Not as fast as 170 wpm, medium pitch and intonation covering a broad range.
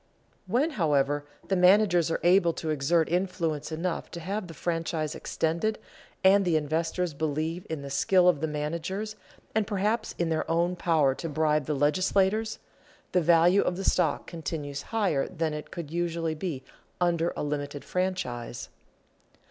No: average, 155 wpm; medium, 165 Hz; average, 3.3 semitones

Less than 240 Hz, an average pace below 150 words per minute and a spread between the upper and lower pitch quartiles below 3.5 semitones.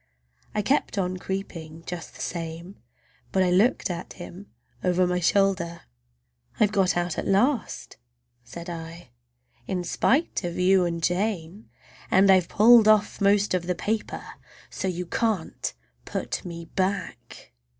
Yes: medium, 185 Hz; average, 140 wpm; average, 2.7 semitones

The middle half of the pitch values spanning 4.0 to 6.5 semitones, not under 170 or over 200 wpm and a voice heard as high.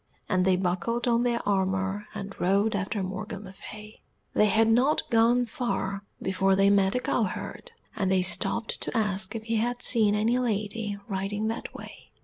No: average, 2.9 semitones; average, 175 wpm; high, 210 Hz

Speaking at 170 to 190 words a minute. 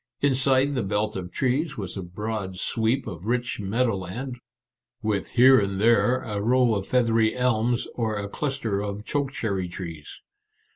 No: average, 160 wpm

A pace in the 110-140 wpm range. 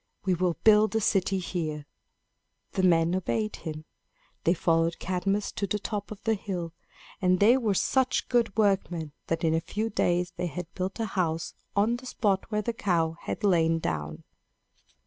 No: average, 175 wpm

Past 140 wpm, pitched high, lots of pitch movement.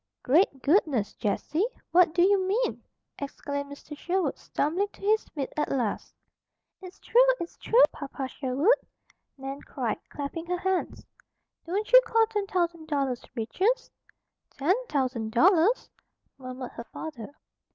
No: slow, 135 wpm; very high, 315 Hz; wide, 5.9 semitones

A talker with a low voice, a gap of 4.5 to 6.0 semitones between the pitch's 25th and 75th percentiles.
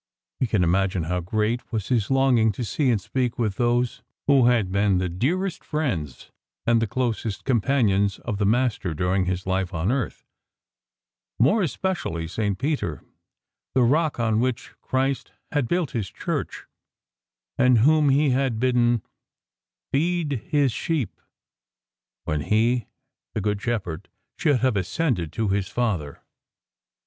Yes: low, 115 Hz; average, 5.2 semitones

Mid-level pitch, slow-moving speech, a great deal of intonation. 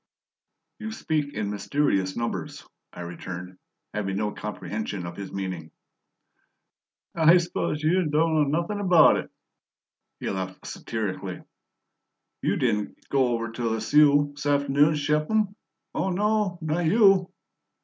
Yes: medium, 145 Hz; slow, 130 wpm; wide, 8.1 semitones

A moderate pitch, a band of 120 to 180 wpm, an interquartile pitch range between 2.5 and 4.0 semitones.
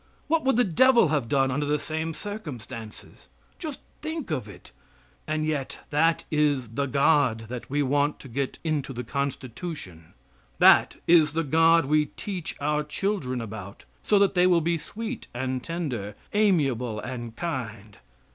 No: medium, 145 Hz; average, 155 wpm; average, 4.9 semitones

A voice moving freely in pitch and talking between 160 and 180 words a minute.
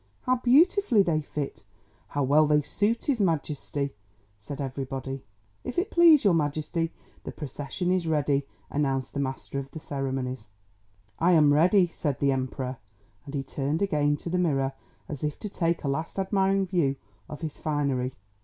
No: average, 4.7 semitones; average, 165 wpm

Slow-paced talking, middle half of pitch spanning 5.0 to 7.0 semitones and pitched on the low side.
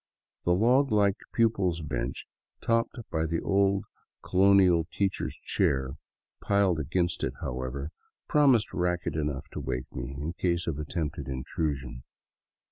Yes: slow, 125 wpm; wide, 5.5 semitones; very low, 85 Hz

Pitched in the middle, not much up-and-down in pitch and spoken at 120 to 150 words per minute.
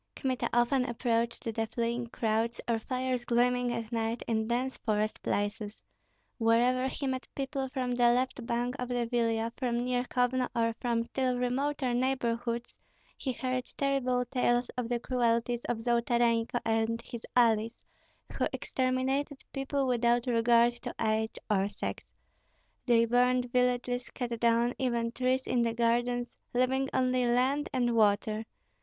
No: high, 240 Hz; narrow, 1.6 semitones; average, 145 wpm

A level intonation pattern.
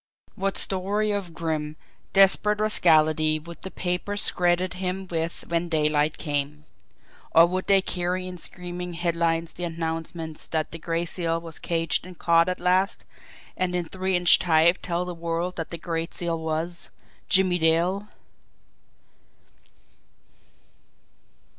Yes: narrow, 2.0 semitones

